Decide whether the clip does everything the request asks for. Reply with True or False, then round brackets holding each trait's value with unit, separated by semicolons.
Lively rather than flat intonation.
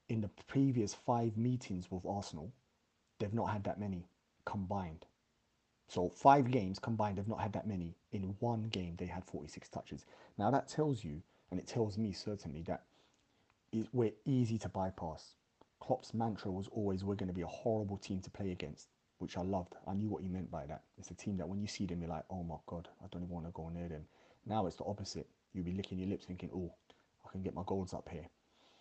False (3.4 semitones)